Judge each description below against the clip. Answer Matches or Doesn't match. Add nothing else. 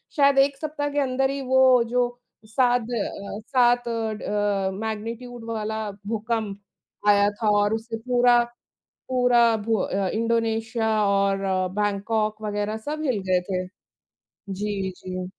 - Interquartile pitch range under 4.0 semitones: Matches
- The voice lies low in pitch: Doesn't match